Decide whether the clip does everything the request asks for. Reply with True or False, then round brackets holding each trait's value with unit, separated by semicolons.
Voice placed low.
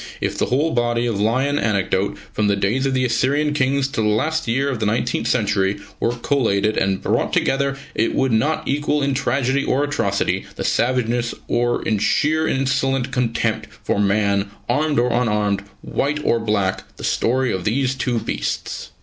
True (120 Hz)